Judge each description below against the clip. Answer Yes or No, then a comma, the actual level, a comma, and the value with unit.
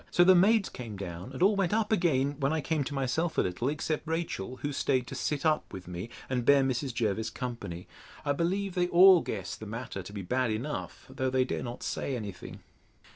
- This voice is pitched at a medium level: No, low, 130 Hz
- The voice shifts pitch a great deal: Yes, wide, 6.3 semitones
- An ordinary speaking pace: No, fast, 225 wpm